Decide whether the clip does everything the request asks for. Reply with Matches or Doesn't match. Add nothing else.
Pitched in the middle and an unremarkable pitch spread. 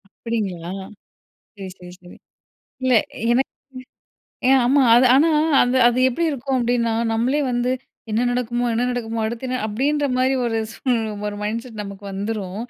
Doesn't match